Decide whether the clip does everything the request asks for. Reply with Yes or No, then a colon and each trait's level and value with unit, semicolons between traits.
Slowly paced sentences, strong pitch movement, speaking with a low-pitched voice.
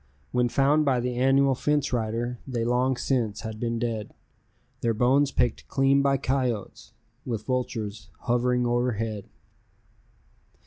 No: slow, 130 wpm; narrow, 2.6 semitones; low, 125 Hz